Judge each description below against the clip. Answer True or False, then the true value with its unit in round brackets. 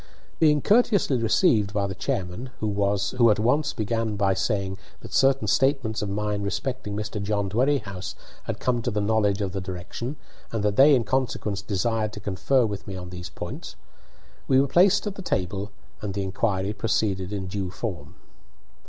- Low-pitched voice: True (105 Hz)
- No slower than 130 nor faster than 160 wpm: False (175 wpm)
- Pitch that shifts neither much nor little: True (3.8 semitones)